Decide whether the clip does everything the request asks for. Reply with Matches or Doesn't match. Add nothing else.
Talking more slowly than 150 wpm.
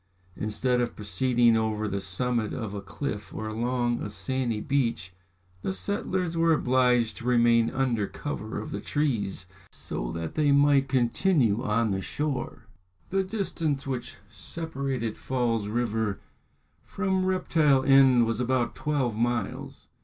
Matches